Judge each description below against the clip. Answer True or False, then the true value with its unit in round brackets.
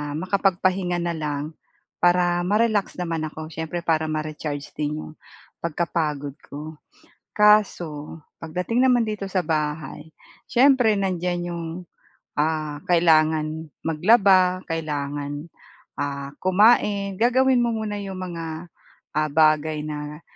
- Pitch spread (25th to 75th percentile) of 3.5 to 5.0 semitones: True (3.8 semitones)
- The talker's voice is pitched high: False (165 Hz)